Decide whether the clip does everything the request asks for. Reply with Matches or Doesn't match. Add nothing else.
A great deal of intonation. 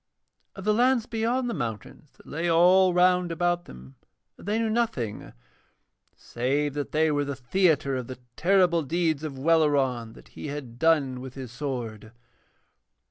Matches